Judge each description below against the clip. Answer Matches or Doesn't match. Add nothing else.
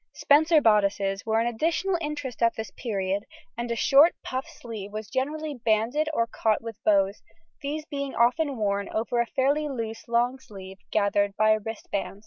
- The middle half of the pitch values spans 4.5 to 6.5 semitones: Matches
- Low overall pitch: Doesn't match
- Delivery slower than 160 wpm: Doesn't match